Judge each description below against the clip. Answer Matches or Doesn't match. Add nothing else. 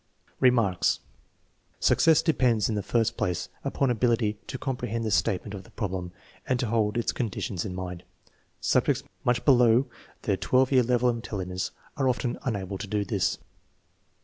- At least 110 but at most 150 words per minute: Doesn't match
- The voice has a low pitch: Matches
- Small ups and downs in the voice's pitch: Doesn't match